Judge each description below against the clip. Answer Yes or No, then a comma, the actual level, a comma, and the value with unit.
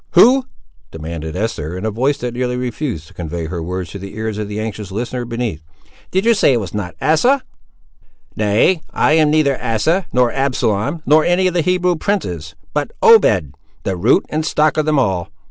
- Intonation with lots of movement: Yes, wide, 8.3 semitones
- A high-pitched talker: No, low, 120 Hz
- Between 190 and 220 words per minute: Yes, average, 195 wpm